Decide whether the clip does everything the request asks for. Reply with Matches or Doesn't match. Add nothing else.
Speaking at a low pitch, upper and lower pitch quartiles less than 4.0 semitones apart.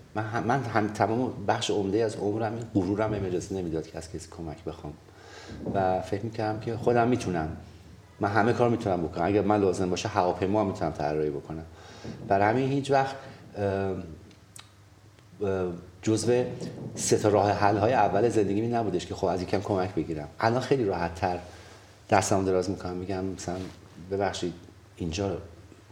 Matches